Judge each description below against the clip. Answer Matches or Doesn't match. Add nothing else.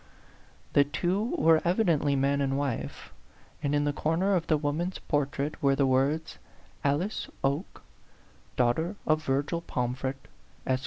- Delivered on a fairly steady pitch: Doesn't match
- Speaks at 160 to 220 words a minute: Doesn't match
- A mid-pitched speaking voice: Matches